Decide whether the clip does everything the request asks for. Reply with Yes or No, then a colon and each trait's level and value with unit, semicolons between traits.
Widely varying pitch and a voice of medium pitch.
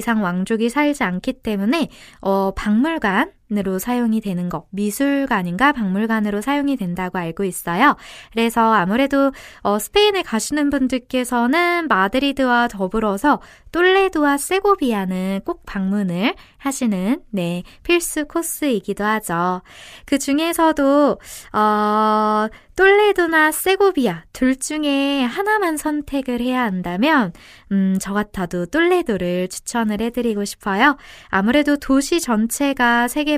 No: wide, 6.3 semitones; high, 240 Hz